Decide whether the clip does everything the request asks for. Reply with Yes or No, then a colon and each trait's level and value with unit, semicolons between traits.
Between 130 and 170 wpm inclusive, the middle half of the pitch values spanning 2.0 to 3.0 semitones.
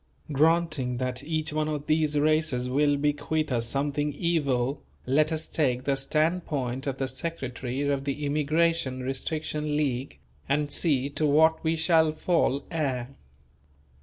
Yes: average, 140 wpm; average, 2.7 semitones